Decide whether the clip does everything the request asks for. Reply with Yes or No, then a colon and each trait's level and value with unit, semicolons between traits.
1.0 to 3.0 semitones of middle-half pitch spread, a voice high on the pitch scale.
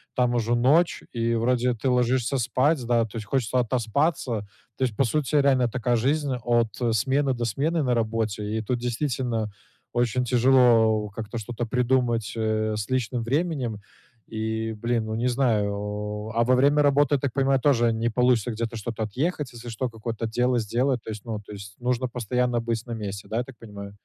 No: narrow, 2.5 semitones; low, 120 Hz